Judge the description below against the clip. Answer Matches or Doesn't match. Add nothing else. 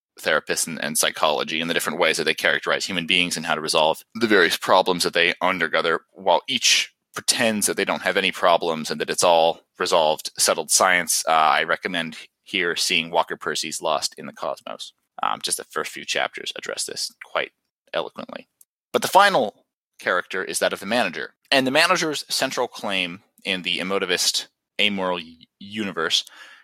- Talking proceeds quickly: Doesn't match